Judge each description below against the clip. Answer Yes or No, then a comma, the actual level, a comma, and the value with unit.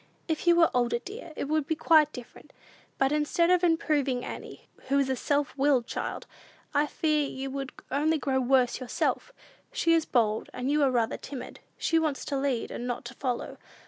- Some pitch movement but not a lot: Yes, average, 3.4 semitones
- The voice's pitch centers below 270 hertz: No, very high, 280 Hz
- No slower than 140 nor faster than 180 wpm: No, average, 195 wpm